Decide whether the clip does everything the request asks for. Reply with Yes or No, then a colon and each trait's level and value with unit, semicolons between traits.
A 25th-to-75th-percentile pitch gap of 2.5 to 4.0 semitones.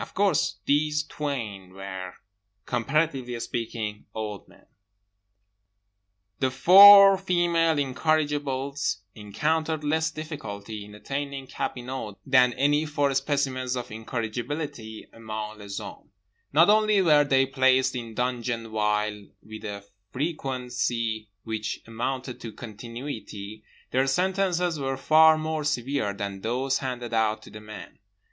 No: average, 5.3 semitones